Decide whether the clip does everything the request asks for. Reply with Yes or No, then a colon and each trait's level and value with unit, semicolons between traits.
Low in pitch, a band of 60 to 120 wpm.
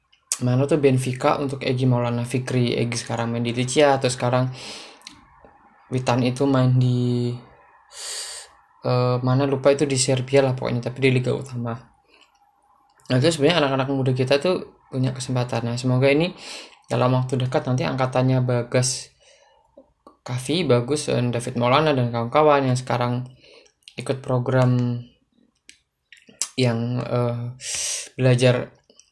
No: low, 125 Hz; average, 130 wpm